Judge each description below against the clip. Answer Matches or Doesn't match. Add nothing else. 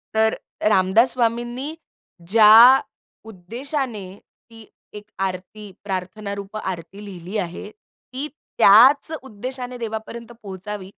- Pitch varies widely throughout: Doesn't match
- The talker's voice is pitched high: Matches